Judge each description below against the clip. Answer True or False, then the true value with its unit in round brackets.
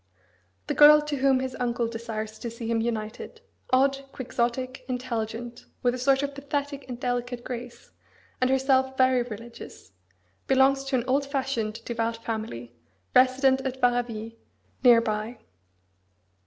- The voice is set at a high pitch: True (250 Hz)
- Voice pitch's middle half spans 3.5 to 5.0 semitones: False (2.4 semitones)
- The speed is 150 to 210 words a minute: False (140 wpm)